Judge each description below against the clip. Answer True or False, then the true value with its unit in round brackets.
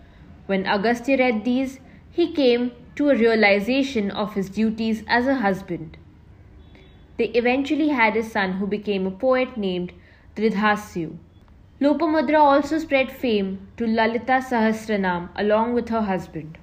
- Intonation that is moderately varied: True (4.9 semitones)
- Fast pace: False (135 wpm)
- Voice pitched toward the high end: True (220 Hz)